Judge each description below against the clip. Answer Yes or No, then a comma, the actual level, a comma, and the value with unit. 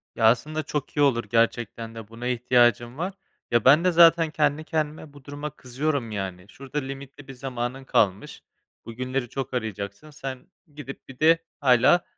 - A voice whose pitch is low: Yes, low, 130 Hz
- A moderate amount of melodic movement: Yes, average, 3.9 semitones